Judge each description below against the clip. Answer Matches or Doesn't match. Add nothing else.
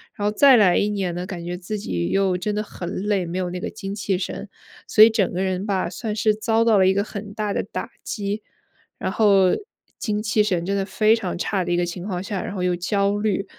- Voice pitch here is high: Matches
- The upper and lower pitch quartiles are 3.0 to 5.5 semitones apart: Doesn't match